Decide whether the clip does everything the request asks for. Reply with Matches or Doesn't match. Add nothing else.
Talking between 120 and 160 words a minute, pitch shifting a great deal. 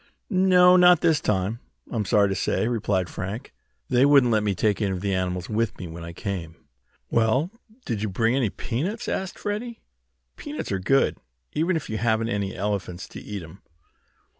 Doesn't match